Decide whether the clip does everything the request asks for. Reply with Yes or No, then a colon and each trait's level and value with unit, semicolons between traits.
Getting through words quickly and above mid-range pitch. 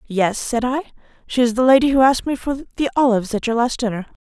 Yes: fast, 240 wpm; high, 245 Hz